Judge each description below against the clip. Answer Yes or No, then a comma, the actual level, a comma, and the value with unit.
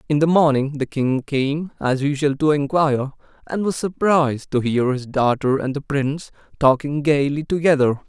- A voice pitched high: No, medium, 145 Hz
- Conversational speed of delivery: Yes, average, 170 wpm